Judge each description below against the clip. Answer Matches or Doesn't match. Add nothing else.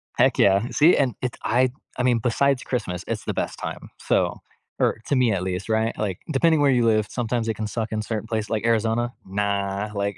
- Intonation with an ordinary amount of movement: Matches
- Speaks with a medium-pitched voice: Doesn't match